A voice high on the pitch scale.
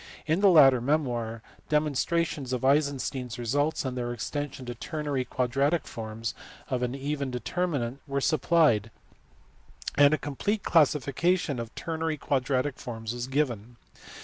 No: low, 135 Hz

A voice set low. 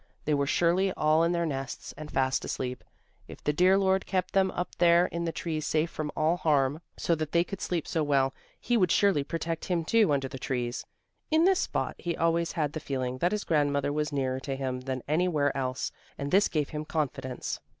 No: medium, 155 Hz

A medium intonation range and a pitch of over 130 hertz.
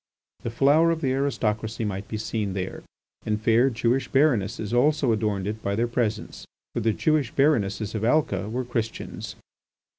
No: average, 4.0 semitones; low, 115 Hz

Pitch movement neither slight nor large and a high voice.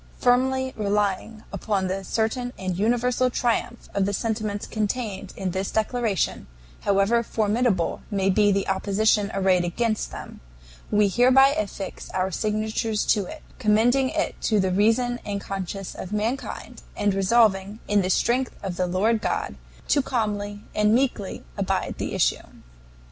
Yes: average, 3.3 semitones; high, 210 Hz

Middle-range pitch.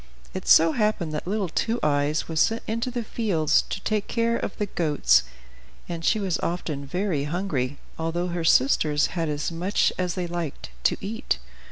Yes: medium, 175 Hz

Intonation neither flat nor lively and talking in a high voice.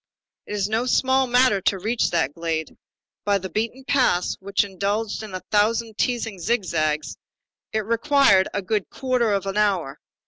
Yes: average, 3.7 semitones; high, 205 Hz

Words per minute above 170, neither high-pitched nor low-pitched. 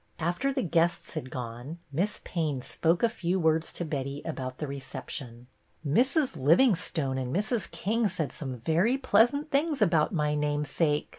No: average, 165 wpm; medium, 160 Hz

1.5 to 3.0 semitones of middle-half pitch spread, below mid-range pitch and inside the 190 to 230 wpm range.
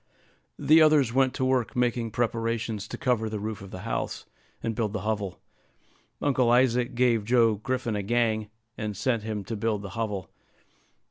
No: narrow, 2.6 semitones; low, 115 Hz; average, 175 wpm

